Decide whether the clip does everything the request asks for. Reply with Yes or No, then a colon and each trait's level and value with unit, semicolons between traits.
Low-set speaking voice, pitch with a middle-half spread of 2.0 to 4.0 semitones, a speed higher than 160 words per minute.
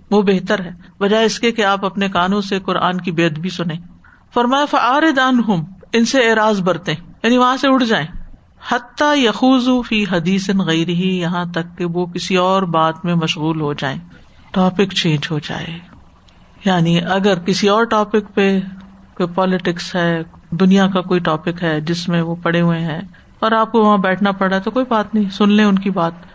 No: high, 190 Hz; average, 3.7 semitones; average, 185 wpm